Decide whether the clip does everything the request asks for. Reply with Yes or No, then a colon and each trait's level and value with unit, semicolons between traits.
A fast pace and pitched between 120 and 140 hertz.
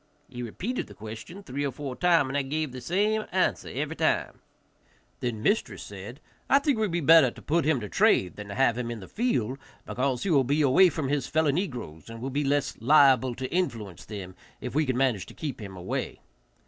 Yes: fast, 225 wpm; low, 135 Hz